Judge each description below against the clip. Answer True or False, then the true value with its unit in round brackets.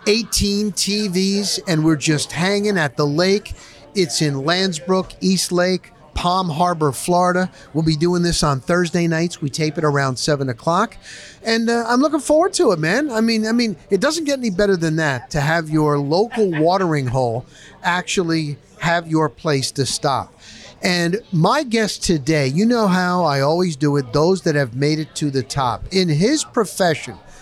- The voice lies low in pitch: False (175 Hz)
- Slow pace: False (180 wpm)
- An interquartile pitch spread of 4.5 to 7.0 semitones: True (4.8 semitones)